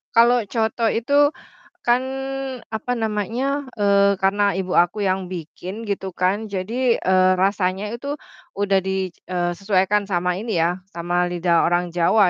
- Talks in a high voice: Yes, high, 195 Hz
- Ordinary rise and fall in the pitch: Yes, average, 3.1 semitones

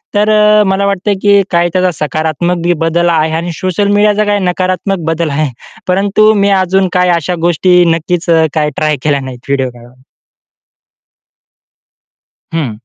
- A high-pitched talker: No, medium, 175 Hz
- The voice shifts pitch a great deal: No, average, 3.8 semitones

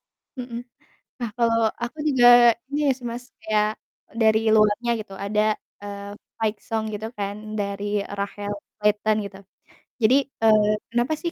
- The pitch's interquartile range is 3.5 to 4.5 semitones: No, narrow, 2.5 semitones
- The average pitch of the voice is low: No, high, 220 Hz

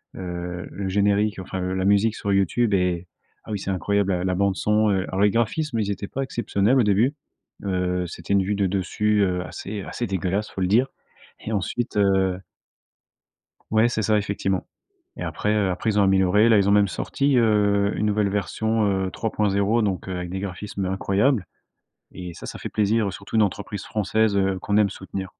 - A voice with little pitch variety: Yes, narrow, 2.0 semitones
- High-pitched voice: No, low, 100 Hz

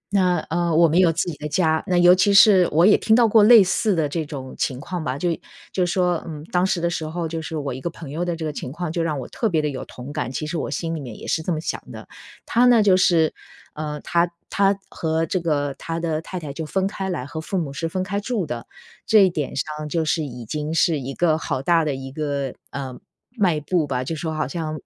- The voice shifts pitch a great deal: No, average, 3.1 semitones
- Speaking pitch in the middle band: Yes, medium, 160 Hz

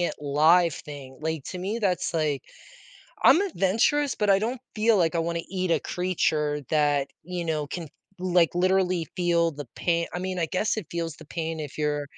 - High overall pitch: No, medium, 170 Hz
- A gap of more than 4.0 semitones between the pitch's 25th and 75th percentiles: No, average, 3.2 semitones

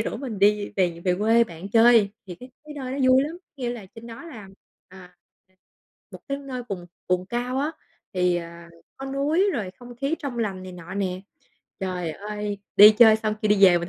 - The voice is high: Yes, high, 215 Hz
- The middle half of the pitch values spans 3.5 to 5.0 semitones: No, wide, 5.4 semitones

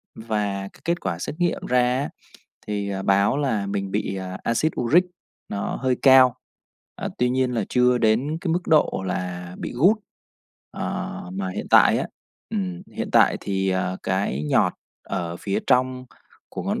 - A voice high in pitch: No, low, 110 Hz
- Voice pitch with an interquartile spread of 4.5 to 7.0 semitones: Yes, average, 4.9 semitones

